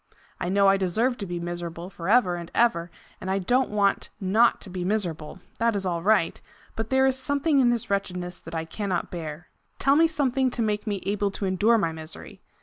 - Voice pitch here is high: Yes, high, 195 Hz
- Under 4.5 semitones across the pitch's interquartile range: No, average, 4.9 semitones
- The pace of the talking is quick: Yes, fast, 215 wpm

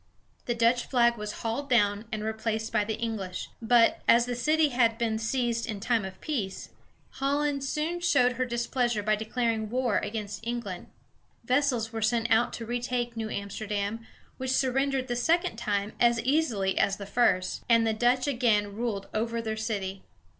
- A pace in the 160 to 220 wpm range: Yes, average, 170 wpm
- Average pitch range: No, narrow, 2.3 semitones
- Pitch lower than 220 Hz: No, high, 230 Hz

